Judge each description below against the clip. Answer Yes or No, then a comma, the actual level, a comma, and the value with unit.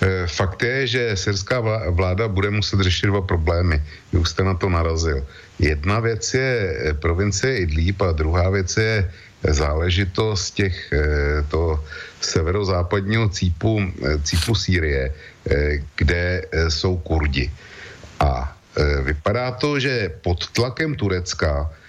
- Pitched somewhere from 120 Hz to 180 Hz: No, very low, 95 Hz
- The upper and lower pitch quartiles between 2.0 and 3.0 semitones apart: No, average, 4.4 semitones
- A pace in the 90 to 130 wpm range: Yes, slow, 110 wpm